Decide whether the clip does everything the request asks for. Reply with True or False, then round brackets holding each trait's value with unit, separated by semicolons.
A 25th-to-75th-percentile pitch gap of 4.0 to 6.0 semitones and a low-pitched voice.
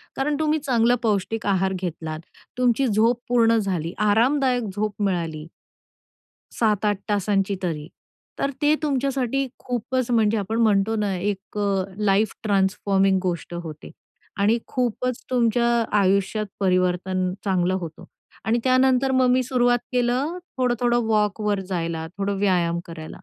False (4.3 semitones; 210 Hz)